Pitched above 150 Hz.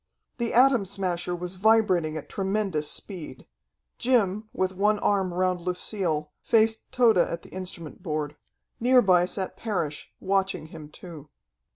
Yes: medium, 185 Hz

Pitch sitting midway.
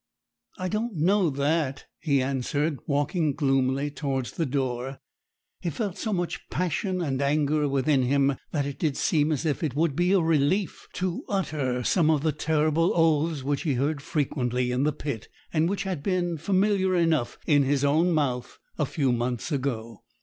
Yes: medium, 150 Hz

